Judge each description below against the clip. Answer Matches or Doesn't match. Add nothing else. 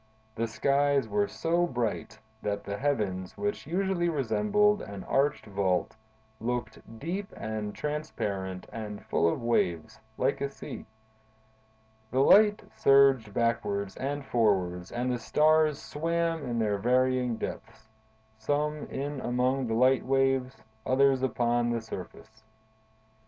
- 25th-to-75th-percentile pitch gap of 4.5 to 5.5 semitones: Matches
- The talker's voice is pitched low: Matches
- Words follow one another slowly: Matches